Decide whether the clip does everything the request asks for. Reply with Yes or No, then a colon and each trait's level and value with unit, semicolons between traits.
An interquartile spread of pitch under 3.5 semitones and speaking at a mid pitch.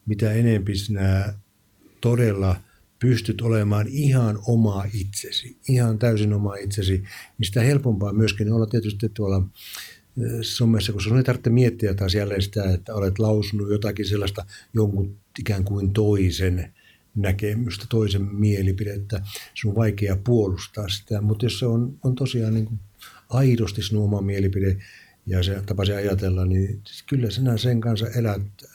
No: narrow, 2.4 semitones; low, 105 Hz